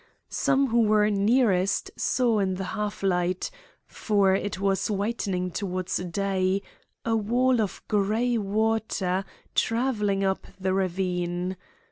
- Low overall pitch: No, high, 200 Hz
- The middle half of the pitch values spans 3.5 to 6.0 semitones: No, average, 2.9 semitones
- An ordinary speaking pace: No, slow, 120 wpm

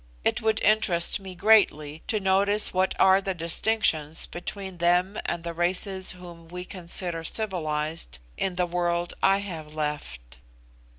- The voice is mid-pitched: Yes, medium, 175 Hz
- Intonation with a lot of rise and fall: No, average, 2.7 semitones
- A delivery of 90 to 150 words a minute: Yes, average, 140 wpm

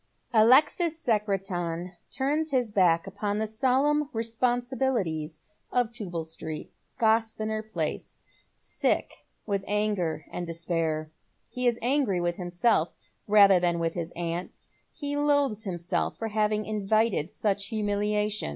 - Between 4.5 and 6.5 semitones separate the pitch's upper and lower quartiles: Yes, average, 5.2 semitones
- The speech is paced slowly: Yes, slow, 120 wpm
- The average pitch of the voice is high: Yes, high, 210 Hz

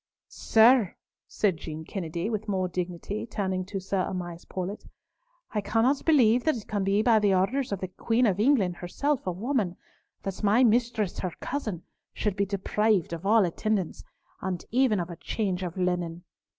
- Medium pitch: No, high, 200 Hz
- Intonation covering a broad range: No, average, 3.7 semitones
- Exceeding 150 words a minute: Yes, average, 175 wpm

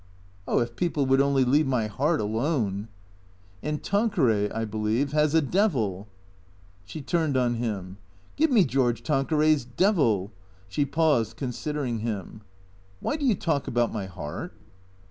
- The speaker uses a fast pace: No, average, 170 wpm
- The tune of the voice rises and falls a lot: Yes, wide, 6.8 semitones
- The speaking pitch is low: Yes, low, 120 Hz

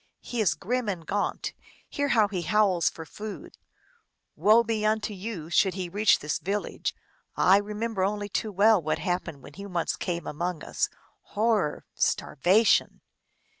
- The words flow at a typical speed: Yes, average, 160 wpm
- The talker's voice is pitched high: Yes, high, 200 Hz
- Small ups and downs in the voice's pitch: No, average, 3.5 semitones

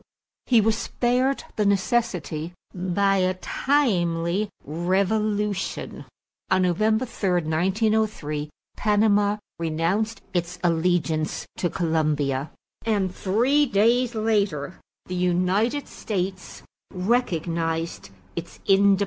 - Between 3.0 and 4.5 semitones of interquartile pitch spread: Yes, average, 4.1 semitones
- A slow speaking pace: Yes, slow, 90 wpm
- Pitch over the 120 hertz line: Yes, high, 190 Hz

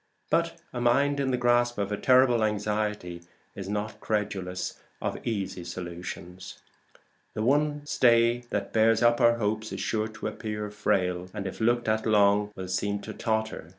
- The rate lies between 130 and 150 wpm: No, average, 165 wpm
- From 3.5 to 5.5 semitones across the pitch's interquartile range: No, average, 2.7 semitones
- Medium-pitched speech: No, low, 110 Hz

